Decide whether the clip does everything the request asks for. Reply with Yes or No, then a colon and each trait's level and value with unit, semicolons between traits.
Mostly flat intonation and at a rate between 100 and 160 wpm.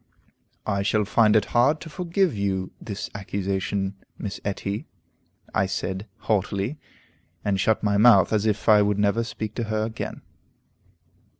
Yes: narrow, 2.1 semitones; average, 145 wpm